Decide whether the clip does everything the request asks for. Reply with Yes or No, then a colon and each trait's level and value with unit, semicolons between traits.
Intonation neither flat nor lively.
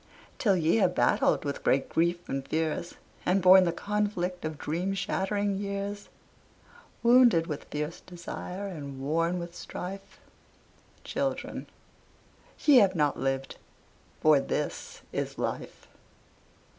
Yes: average, 4.0 semitones